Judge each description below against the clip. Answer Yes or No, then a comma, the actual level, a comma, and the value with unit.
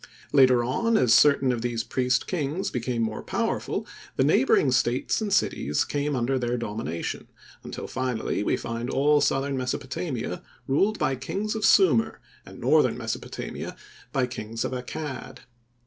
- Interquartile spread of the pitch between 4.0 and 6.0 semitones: No, average, 3.3 semitones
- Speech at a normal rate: Yes, average, 150 wpm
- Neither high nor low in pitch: No, low, 130 Hz